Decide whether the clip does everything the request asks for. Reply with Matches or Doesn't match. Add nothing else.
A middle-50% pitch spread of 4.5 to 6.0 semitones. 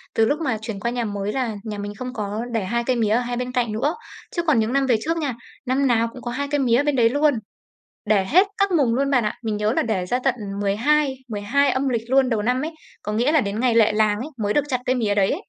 Doesn't match